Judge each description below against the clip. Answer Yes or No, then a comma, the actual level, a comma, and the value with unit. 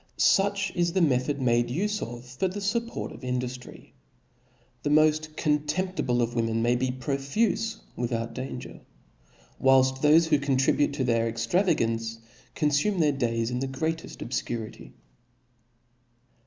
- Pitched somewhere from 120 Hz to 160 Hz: Yes, low, 135 Hz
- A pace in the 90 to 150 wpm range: Yes, slow, 135 wpm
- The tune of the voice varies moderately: Yes, average, 5.0 semitones